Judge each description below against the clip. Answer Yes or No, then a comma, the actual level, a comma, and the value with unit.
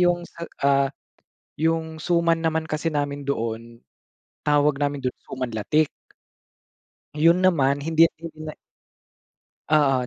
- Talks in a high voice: No, medium, 150 Hz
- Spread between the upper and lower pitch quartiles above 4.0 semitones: No, average, 2.9 semitones